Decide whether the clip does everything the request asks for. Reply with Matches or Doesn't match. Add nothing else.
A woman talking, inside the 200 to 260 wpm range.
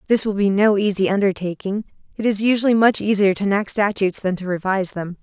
Matches